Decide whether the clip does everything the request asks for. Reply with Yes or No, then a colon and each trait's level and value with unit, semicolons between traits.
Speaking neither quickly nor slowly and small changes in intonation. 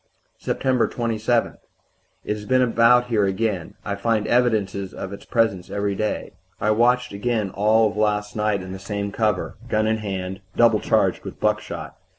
Yes: average, 165 wpm; narrow, 2.3 semitones